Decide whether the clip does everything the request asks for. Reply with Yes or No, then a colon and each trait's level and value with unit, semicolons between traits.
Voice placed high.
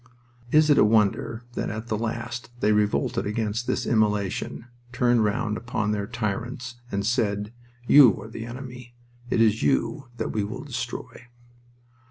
No: low, 115 Hz